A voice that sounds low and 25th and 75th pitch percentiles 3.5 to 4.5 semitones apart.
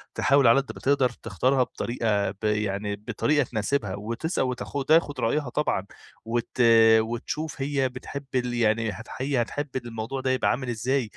Yes: low, 120 Hz; average, 3.8 semitones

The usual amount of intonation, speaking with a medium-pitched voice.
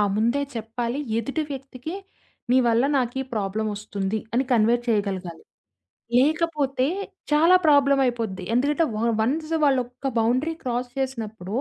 No: average, 4.1 semitones; high, 245 Hz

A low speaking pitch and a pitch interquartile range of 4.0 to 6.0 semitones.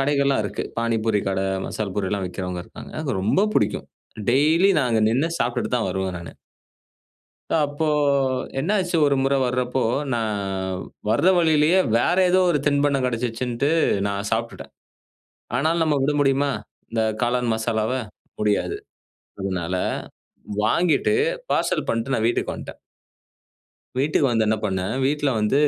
Yes: low, 125 Hz; average, 4.9 semitones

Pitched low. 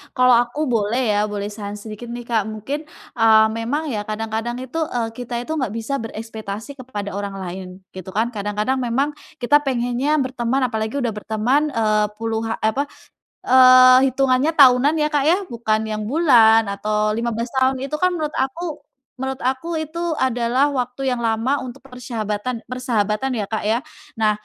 No: high, 240 Hz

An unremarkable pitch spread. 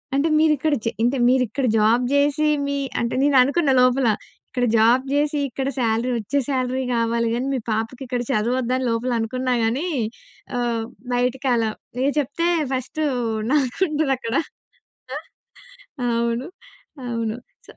Yes: average, 3.1 semitones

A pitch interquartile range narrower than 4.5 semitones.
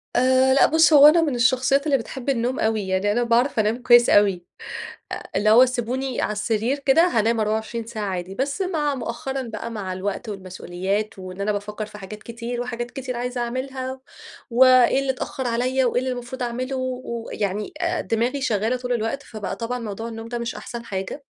Yes: average, 3.3 semitones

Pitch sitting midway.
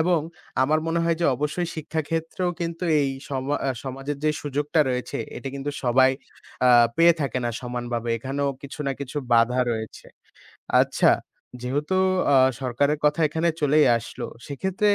Yes: medium, 145 Hz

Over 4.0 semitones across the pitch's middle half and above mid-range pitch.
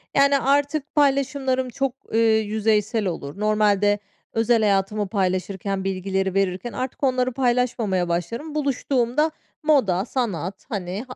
Yes: average, 5.2 semitones; high, 220 Hz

